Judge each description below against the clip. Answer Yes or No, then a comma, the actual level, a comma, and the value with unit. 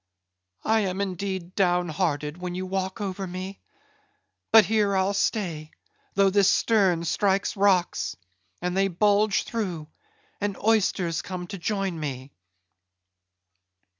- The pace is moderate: No, slow, 125 wpm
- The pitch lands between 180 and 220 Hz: Yes, high, 190 Hz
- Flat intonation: Yes, narrow, 2.2 semitones